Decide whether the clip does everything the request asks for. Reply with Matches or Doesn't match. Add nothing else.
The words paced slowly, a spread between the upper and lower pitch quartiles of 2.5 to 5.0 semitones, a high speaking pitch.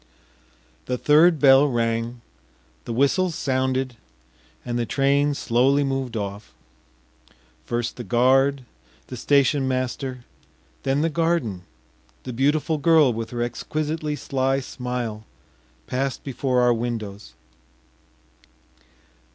Doesn't match